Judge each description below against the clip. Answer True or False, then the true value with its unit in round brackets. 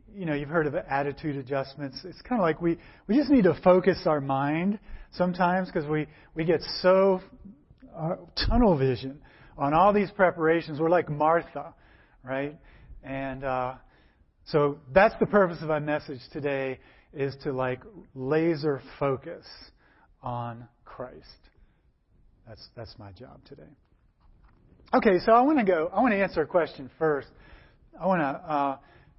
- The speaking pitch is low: False (150 Hz)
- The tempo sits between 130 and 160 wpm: True (155 wpm)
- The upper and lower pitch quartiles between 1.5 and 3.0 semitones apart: False (4.9 semitones)